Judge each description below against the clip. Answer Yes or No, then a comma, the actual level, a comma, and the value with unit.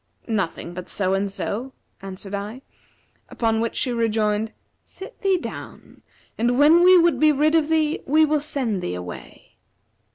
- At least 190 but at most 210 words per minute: No, average, 160 wpm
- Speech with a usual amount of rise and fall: No, wide, 7.2 semitones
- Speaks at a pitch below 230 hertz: No, high, 235 Hz